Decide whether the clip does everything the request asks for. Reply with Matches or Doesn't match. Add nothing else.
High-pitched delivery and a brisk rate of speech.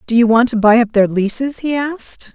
Matches